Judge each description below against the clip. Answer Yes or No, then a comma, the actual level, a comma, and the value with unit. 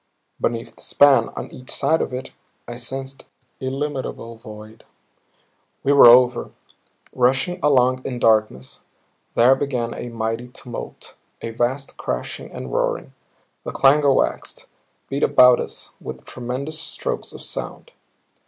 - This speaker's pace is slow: Yes, slow, 130 wpm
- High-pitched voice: No, low, 125 Hz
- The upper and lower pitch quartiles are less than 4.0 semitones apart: Yes, average, 2.8 semitones